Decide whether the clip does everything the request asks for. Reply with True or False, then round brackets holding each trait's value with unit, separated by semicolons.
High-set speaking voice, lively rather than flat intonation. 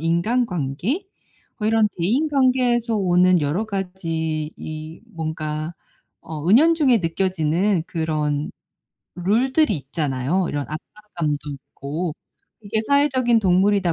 False (180 Hz; 6.2 semitones)